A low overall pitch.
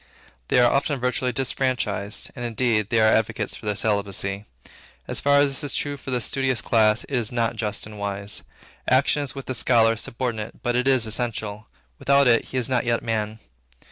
Yes: low, 120 Hz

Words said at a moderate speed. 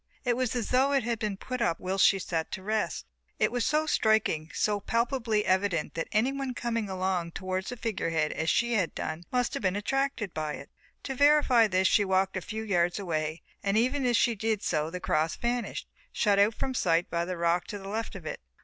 No: fast, 220 wpm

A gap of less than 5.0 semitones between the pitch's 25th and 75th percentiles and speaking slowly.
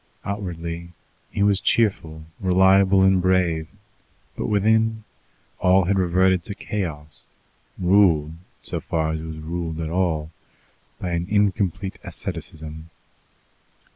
Yes: average, 3.3 semitones; slow, 115 wpm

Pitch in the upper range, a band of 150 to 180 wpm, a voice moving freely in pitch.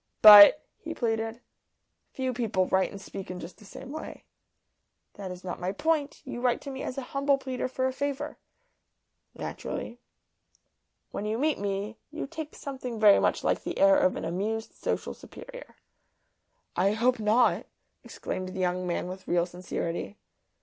Yes: high, 225 Hz; average, 165 wpm; wide, 6.2 semitones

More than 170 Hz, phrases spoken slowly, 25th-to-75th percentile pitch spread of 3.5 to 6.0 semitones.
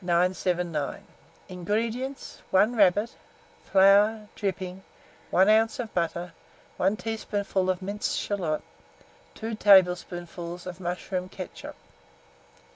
No: high, 190 Hz; slow, 95 wpm; average, 2.9 semitones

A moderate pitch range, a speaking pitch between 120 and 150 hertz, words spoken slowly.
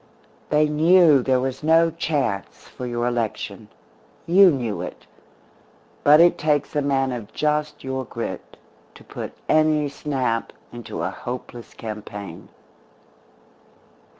Yes: average, 4.1 semitones; low, 135 Hz; slow, 125 wpm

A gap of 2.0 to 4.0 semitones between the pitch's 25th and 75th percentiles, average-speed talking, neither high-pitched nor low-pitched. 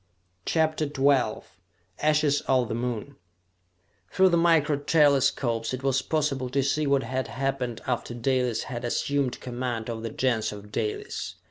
No: average, 3.0 semitones; average, 145 wpm; low, 130 Hz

